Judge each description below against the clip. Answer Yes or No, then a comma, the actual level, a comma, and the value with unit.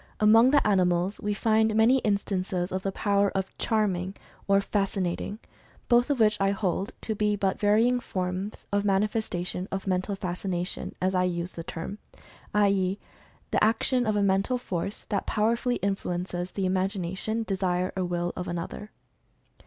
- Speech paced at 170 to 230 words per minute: No, average, 160 wpm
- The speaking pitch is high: Yes, high, 195 Hz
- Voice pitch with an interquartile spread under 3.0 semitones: Yes, narrow, 2.6 semitones